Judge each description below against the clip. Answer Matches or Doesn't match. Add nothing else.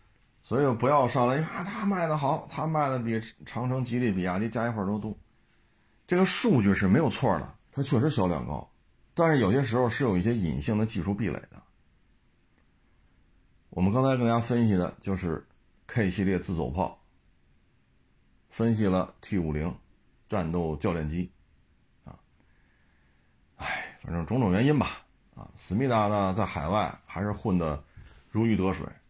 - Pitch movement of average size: Doesn't match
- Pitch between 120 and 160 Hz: Doesn't match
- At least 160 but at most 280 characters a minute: Matches